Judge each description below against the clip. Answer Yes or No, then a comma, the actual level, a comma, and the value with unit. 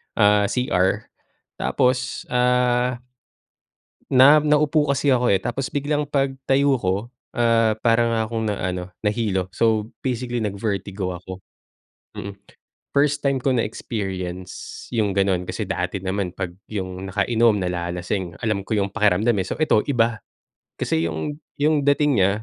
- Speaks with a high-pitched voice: No, low, 110 Hz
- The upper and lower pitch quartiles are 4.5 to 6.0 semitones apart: Yes, average, 5.0 semitones